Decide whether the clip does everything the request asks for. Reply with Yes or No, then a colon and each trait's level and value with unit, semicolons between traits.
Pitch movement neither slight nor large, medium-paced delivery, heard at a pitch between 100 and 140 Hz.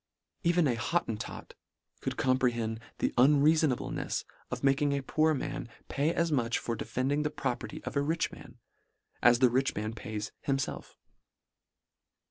Yes: average, 4.1 semitones; average, 145 wpm; low, 135 Hz